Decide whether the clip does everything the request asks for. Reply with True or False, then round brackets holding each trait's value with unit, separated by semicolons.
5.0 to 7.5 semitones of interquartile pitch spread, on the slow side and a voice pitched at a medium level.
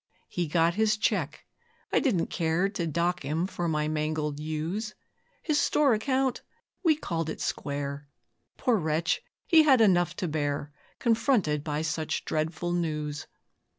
False (5.6 semitones; 145 wpm; 165 Hz)